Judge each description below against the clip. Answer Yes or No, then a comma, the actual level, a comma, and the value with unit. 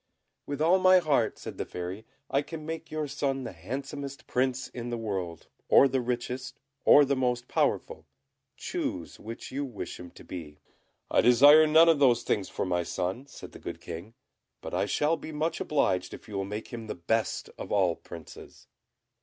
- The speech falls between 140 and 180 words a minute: No, average, 190 wpm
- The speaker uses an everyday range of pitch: No, wide, 6.3 semitones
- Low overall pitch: Yes, low, 125 Hz